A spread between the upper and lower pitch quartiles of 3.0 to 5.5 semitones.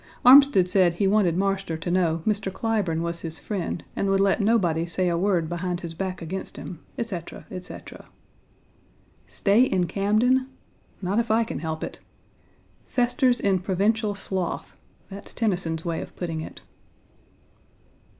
Yes: average, 3.7 semitones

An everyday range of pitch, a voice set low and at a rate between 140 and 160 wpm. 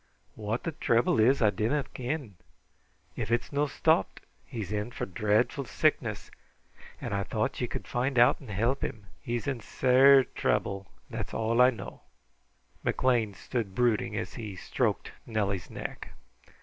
Yes: average, 3.6 semitones; low, 115 Hz; average, 155 wpm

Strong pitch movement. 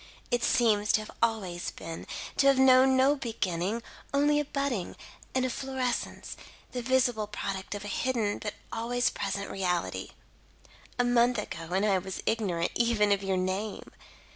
No: average, 4.5 semitones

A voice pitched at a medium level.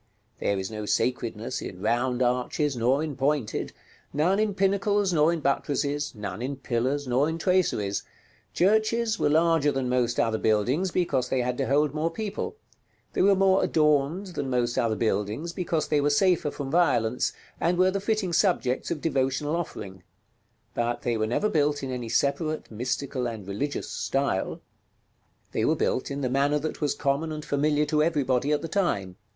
Yes: medium, 145 Hz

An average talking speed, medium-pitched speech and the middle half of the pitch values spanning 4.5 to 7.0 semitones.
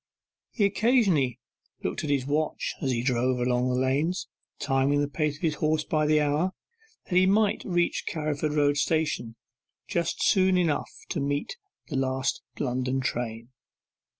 No: average, 155 wpm; medium, 145 Hz; average, 3.9 semitones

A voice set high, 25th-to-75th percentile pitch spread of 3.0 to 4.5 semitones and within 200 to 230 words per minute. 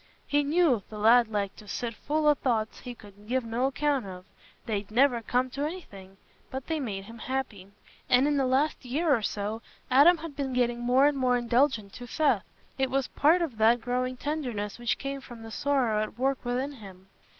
Yes: very high, 250 Hz; average, 4.0 semitones; fast, 205 wpm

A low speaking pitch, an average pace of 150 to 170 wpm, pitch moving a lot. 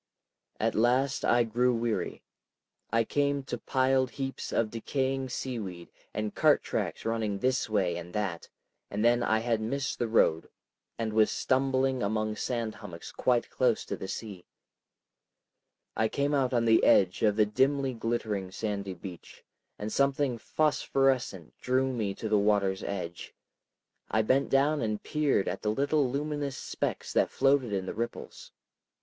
No: low, 115 Hz; average, 155 wpm; average, 4.1 semitones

